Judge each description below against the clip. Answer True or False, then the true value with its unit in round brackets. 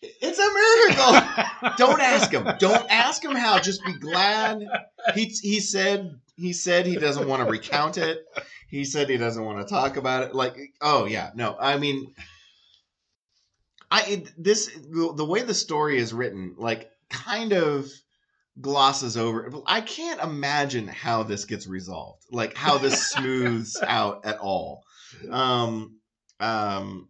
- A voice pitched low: False (145 Hz)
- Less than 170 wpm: True (150 wpm)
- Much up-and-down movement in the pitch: True (9.0 semitones)